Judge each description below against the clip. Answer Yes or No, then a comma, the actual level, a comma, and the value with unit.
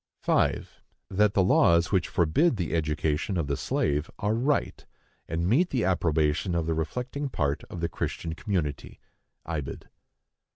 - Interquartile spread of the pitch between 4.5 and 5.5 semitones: Yes, average, 4.9 semitones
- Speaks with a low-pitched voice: Yes, very low, 85 Hz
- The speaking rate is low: No, average, 150 wpm